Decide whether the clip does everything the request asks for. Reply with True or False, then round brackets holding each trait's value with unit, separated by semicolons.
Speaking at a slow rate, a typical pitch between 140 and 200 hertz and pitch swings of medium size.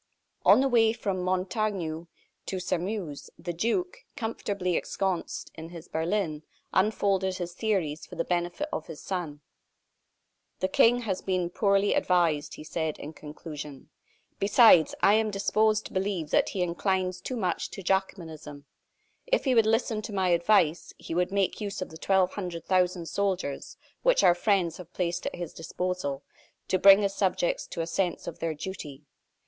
False (165 wpm; 185 Hz; 3.4 semitones)